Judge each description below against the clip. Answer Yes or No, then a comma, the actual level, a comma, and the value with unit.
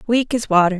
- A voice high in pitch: Yes, high, 215 Hz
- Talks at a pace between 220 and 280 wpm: Yes, fast, 230 wpm